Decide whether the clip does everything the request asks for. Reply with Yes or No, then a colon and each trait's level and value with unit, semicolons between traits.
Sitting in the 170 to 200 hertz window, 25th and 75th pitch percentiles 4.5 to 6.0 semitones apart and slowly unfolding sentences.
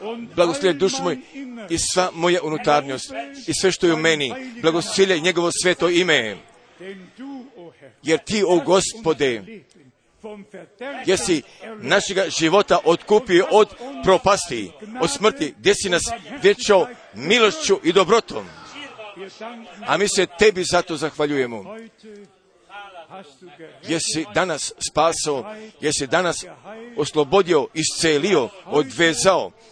Yes: medium, 185 Hz; average, 4.8 semitones; slow, 100 wpm